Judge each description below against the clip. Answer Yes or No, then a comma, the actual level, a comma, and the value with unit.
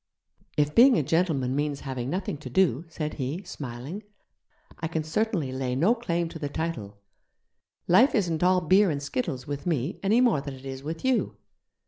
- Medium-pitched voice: Yes, medium, 160 Hz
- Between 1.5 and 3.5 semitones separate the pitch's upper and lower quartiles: No, average, 5.2 semitones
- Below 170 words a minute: No, average, 180 wpm